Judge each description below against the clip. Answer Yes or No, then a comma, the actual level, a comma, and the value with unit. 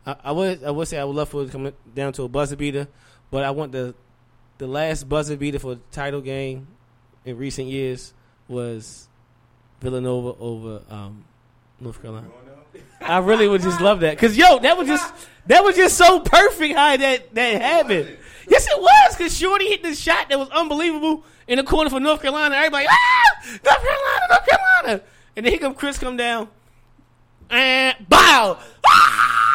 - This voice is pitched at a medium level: Yes, medium, 150 Hz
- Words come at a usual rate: Yes, average, 185 wpm